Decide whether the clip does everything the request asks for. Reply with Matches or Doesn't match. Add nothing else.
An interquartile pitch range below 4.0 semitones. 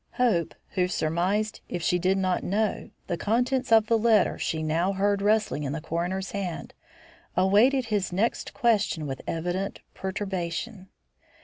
Matches